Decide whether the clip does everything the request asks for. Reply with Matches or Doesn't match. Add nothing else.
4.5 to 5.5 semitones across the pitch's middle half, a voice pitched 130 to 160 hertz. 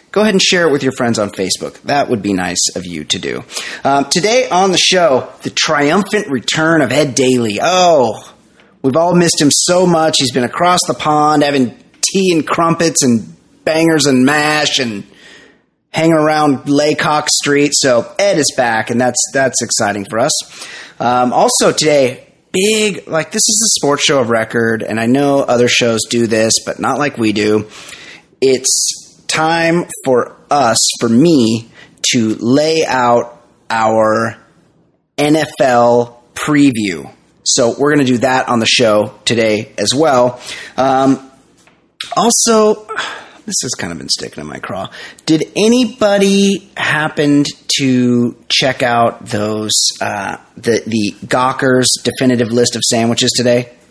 Matches